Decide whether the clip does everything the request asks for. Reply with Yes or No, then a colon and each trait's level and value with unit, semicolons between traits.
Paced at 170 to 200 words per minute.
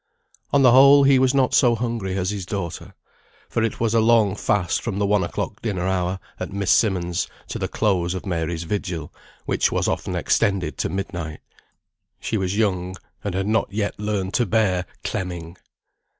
Yes: average, 180 wpm